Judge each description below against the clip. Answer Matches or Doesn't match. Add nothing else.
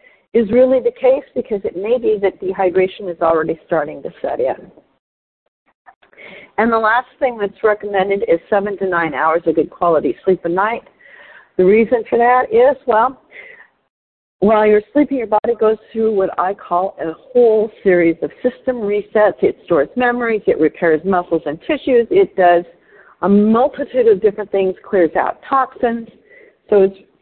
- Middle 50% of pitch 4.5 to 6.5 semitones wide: Matches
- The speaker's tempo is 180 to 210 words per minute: Doesn't match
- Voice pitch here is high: Matches